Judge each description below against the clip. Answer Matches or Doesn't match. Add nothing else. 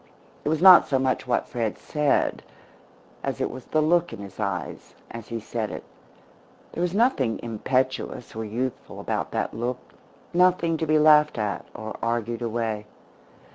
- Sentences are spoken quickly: Doesn't match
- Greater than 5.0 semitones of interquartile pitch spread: Matches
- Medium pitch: Doesn't match